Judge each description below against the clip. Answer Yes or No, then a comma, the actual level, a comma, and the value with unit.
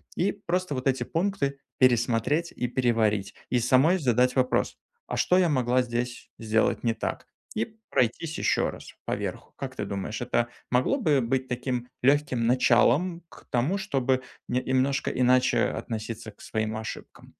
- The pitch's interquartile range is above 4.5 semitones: No, average, 3.1 semitones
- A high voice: No, low, 125 Hz